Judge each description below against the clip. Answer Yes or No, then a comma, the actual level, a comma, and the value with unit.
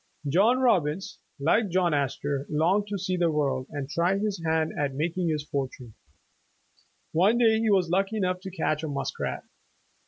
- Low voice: No, medium, 170 Hz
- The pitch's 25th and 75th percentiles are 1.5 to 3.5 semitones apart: No, average, 4.9 semitones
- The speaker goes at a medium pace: Yes, average, 165 wpm